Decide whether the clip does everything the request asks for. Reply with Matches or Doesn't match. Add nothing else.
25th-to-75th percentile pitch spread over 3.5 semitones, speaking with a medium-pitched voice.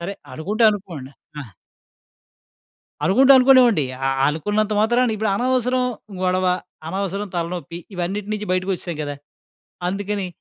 Doesn't match